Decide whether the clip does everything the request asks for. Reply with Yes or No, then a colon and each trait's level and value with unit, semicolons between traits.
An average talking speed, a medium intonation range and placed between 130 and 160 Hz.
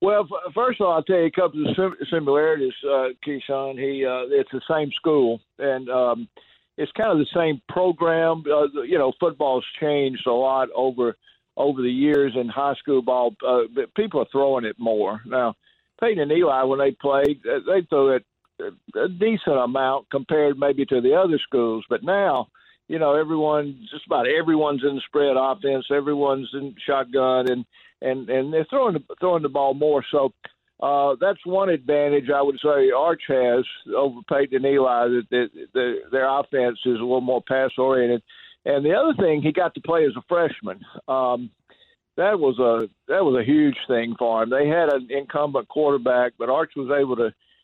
Yes: average, 185 wpm; average, 3.5 semitones; medium, 140 Hz